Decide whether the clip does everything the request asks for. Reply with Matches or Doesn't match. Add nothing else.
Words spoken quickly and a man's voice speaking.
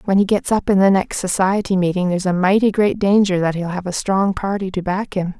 Doesn't match